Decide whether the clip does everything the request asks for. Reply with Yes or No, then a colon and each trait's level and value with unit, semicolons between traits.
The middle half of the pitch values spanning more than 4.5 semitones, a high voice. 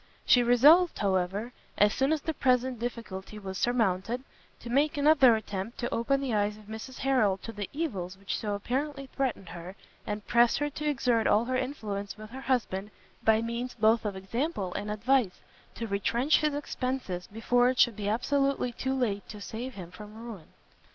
No: average, 4.2 semitones; high, 235 Hz